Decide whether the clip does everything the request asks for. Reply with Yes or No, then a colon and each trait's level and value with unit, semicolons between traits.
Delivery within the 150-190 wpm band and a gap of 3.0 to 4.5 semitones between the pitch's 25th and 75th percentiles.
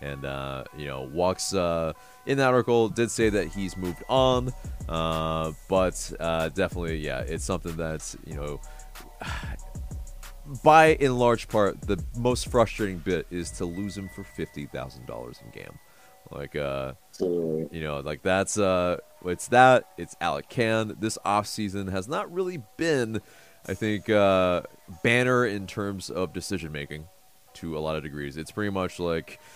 No: average, 160 wpm; average, 5.2 semitones